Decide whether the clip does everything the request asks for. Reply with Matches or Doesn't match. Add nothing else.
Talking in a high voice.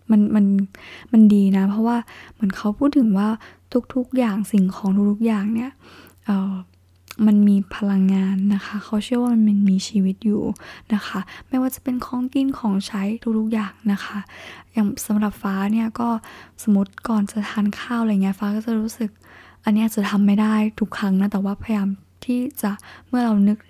Matches